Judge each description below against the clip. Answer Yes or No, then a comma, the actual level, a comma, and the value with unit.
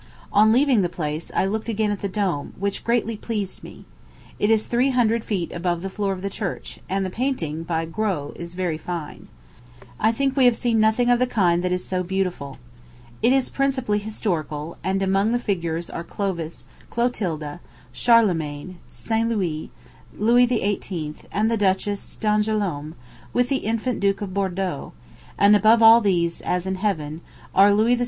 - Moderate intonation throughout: Yes, average, 4.3 semitones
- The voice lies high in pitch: Yes, high, 200 Hz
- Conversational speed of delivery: Yes, average, 175 wpm